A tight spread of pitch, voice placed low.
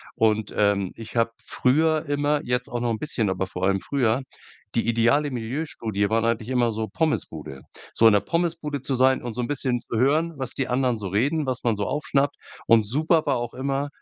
No: average, 4.3 semitones; low, 125 Hz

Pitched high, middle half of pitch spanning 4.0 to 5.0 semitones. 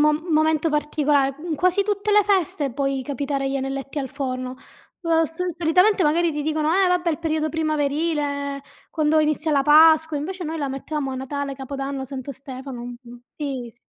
No: very high, 295 Hz; average, 2.8 semitones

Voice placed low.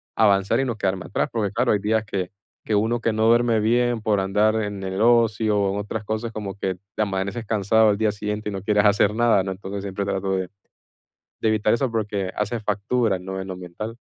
Yes: low, 105 Hz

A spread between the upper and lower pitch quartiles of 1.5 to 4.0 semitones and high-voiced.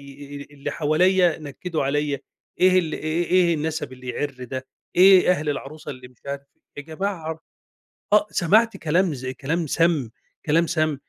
No: average, 3.7 semitones; medium, 155 Hz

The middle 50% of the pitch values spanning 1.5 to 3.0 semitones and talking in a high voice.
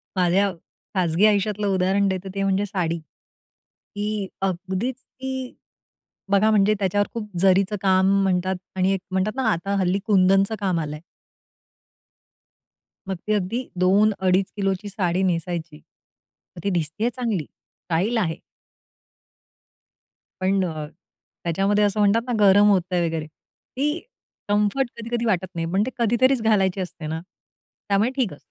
Yes: narrow, 2.4 semitones; high, 195 Hz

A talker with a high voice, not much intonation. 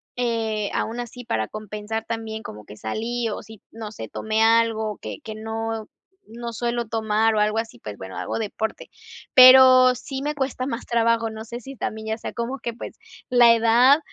Yes: high, 225 Hz; narrow, 1.7 semitones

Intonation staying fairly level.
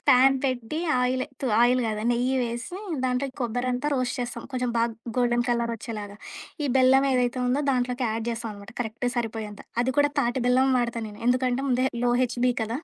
Yes: narrow, 1.6 semitones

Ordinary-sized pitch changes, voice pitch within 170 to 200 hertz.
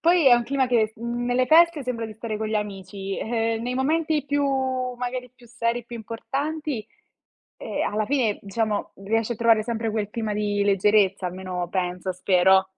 No: average, 3.5 semitones; high, 225 Hz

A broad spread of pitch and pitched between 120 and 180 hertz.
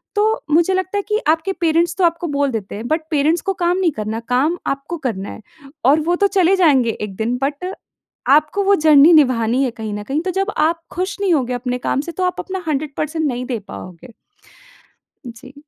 No: wide, 6.0 semitones; very high, 305 Hz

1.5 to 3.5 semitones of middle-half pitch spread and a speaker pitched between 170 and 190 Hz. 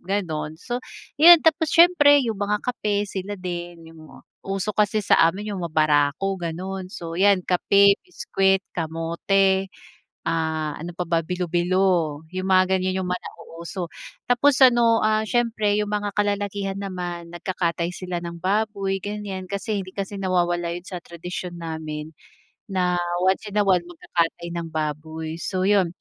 Yes: average, 3.1 semitones; medium, 185 Hz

